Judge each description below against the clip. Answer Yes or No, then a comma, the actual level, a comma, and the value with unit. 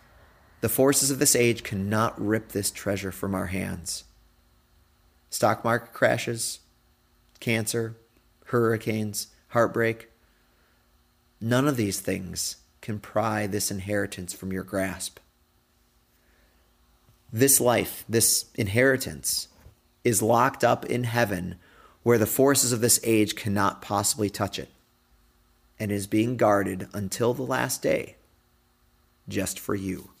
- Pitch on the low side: Yes, low, 105 Hz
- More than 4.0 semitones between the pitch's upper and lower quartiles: No, average, 3.6 semitones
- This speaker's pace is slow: Yes, slow, 115 wpm